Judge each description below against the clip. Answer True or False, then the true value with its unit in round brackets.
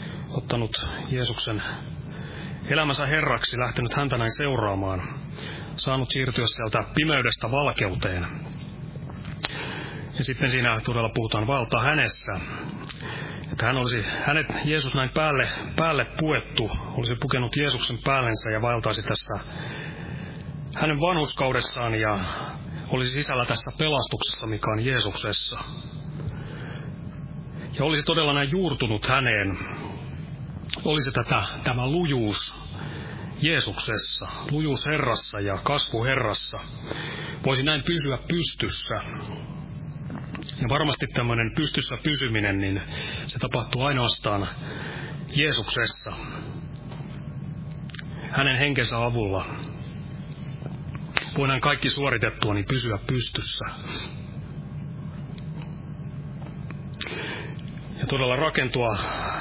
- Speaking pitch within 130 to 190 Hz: True (140 Hz)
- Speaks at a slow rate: True (90 wpm)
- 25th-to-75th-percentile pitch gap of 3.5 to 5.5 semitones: True (4.2 semitones)